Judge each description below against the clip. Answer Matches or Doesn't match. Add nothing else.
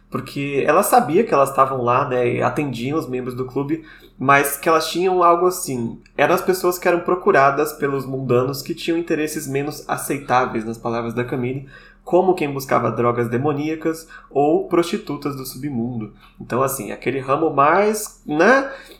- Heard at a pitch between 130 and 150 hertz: Matches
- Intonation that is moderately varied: Matches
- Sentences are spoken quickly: Doesn't match